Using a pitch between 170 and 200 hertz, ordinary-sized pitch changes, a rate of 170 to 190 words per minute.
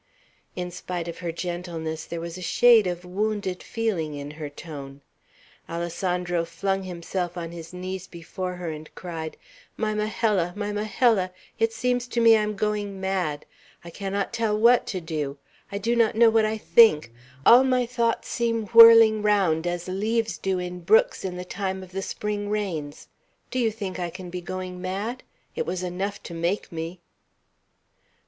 Yes: medium, 185 Hz; average, 3.9 semitones; average, 175 wpm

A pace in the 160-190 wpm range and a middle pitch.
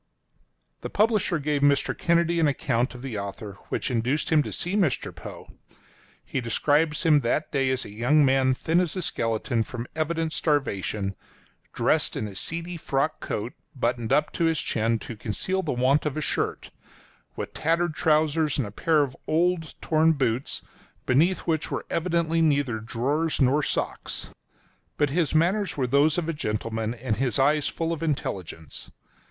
Yes: average, 170 wpm; medium, 145 Hz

